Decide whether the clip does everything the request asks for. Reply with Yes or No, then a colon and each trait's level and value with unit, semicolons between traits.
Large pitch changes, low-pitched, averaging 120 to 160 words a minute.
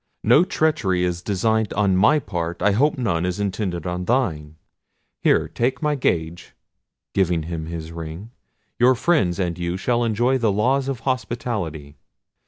Yes: wide, 5.9 semitones; low, 100 Hz; average, 155 wpm